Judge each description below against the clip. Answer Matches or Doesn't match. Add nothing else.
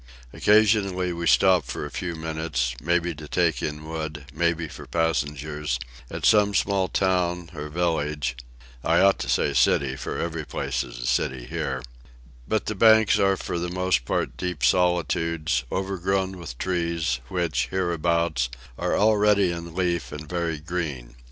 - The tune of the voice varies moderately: Matches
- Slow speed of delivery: Doesn't match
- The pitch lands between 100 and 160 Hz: Doesn't match